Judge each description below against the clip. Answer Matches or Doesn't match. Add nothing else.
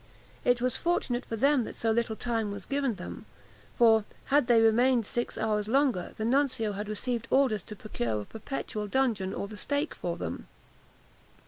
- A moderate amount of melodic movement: Matches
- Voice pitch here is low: Doesn't match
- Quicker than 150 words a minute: Matches